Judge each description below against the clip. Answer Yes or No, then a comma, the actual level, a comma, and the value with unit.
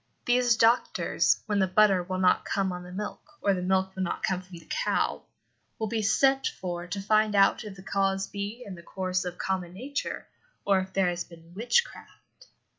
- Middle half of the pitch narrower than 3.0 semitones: Yes, narrow, 2.6 semitones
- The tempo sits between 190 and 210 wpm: Yes, average, 200 wpm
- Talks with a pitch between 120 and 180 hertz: No, high, 195 Hz